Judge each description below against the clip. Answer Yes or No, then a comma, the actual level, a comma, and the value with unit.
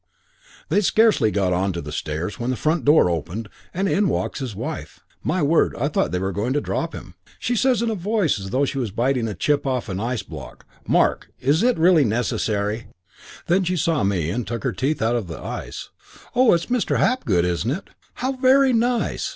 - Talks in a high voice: No, low, 130 Hz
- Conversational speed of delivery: No, fast, 215 wpm